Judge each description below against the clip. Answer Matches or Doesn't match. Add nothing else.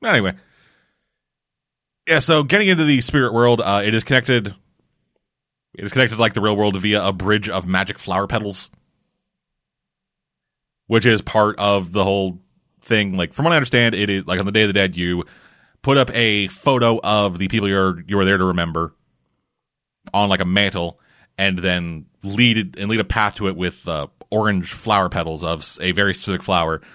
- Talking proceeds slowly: Doesn't match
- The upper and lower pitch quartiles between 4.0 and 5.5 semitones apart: Doesn't match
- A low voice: Matches